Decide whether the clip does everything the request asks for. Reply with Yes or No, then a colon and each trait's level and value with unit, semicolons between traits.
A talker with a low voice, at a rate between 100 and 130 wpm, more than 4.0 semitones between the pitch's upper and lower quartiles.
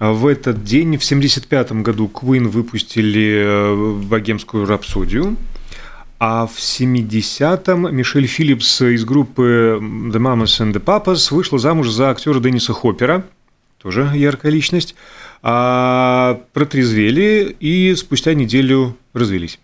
Yes: low, 125 Hz; average, 115 wpm; average, 4.4 semitones